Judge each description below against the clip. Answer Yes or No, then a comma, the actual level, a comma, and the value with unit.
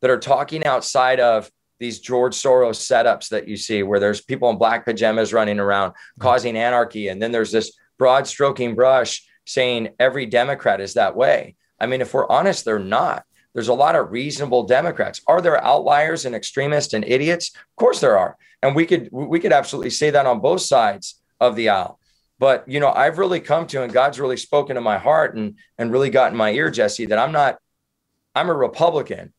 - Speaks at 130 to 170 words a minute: No, fast, 205 wpm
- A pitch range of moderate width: Yes, average, 3.7 semitones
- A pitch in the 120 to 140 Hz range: Yes, low, 125 Hz